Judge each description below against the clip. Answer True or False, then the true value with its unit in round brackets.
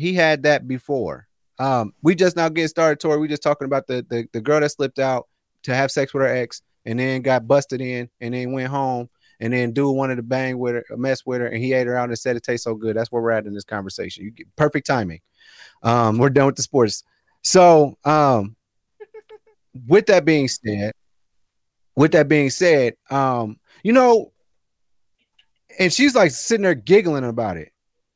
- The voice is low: True (130 Hz)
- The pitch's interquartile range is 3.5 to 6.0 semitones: True (4.0 semitones)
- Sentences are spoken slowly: False (205 wpm)